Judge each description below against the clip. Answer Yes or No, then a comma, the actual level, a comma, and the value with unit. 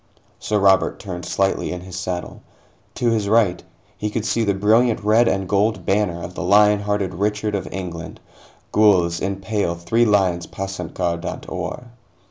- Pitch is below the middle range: Yes, low, 100 Hz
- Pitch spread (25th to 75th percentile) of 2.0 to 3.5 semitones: Yes, average, 2.8 semitones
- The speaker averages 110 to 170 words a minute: Yes, average, 165 wpm